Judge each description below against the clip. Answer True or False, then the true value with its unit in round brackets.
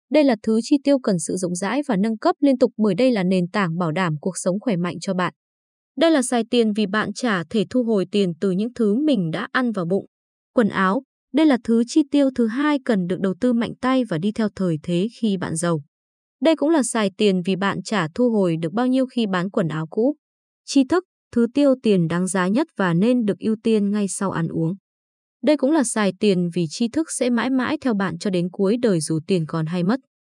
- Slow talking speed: False (250 wpm)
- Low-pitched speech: False (215 Hz)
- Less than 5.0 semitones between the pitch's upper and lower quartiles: False (5.3 semitones)